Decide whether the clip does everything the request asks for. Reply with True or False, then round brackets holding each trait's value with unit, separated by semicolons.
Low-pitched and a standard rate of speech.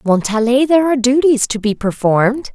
False (245 Hz; 165 wpm)